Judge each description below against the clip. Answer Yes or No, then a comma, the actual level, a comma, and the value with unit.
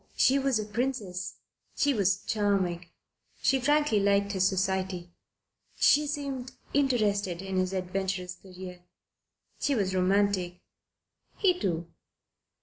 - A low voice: No, high, 200 Hz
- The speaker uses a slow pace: Yes, slow, 115 wpm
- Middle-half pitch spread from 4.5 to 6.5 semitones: Yes, wide, 5.4 semitones